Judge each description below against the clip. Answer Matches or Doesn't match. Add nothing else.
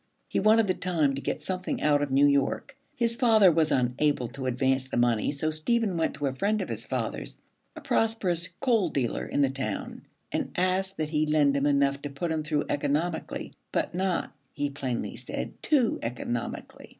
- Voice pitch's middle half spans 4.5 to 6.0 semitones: Matches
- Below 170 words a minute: Doesn't match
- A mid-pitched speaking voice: Matches